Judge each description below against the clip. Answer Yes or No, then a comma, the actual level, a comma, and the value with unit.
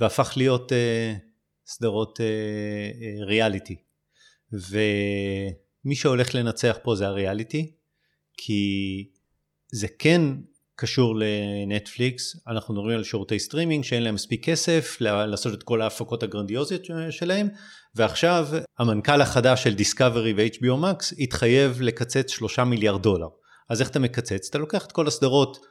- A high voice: No, low, 115 Hz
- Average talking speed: Yes, average, 125 wpm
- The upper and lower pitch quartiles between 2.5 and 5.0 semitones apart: Yes, average, 4.7 semitones